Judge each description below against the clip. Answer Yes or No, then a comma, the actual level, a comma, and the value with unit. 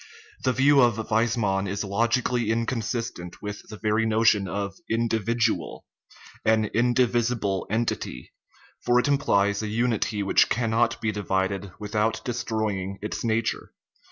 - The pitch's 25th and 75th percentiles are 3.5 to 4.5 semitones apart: No, narrow, 2.4 semitones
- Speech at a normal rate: No, slow, 130 wpm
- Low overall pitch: Yes, low, 110 Hz